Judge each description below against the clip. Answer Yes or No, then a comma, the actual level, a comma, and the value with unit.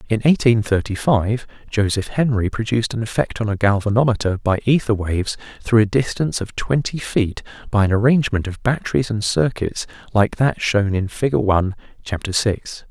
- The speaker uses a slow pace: No, average, 165 wpm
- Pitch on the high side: No, low, 110 Hz